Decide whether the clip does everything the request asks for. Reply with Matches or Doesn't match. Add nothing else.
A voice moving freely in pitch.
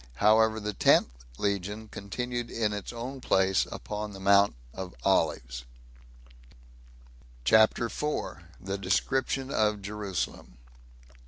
Doesn't match